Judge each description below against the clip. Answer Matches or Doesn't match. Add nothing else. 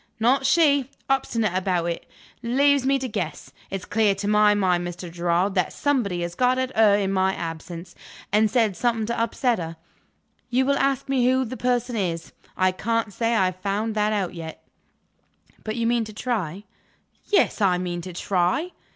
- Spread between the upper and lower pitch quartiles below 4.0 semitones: Doesn't match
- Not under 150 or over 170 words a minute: Doesn't match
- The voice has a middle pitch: Doesn't match